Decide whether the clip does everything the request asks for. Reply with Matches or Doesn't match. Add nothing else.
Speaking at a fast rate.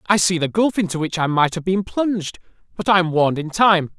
Matches